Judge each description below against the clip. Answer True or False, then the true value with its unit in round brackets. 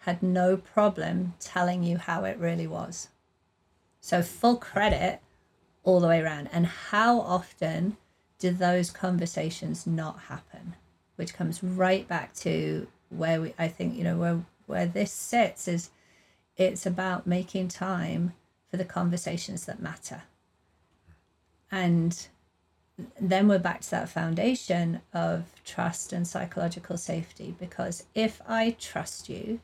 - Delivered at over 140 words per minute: False (135 wpm)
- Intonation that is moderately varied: False (2.3 semitones)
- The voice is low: False (175 Hz)